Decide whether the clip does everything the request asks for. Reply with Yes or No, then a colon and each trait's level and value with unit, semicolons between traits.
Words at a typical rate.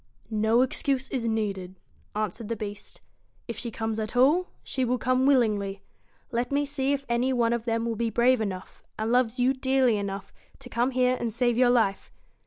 Yes: average, 195 wpm